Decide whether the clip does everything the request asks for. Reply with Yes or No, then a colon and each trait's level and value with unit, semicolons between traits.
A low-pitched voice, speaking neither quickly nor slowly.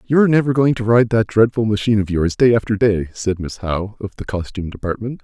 No: low, 110 Hz; fast, 230 wpm